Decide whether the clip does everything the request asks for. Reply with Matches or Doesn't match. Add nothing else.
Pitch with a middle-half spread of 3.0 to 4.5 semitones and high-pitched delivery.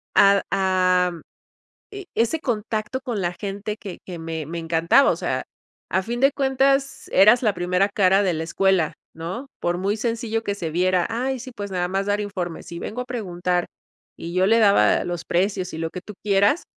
Matches